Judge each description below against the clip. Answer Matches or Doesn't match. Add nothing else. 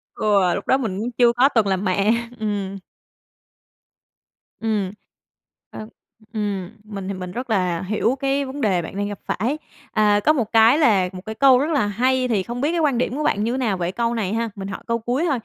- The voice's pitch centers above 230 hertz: Doesn't match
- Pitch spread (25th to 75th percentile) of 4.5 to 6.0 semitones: Doesn't match